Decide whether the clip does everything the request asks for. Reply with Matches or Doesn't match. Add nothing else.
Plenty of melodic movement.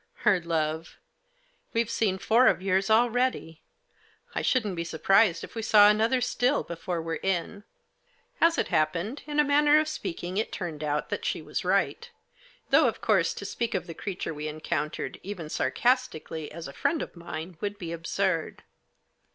Matches